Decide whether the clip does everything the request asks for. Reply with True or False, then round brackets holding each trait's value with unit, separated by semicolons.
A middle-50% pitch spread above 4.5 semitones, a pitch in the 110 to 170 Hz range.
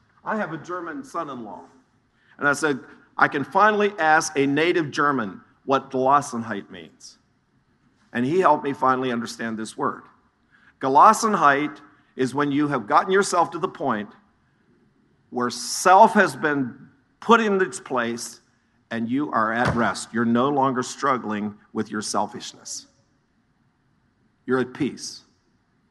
True (5.5 semitones; 140 Hz)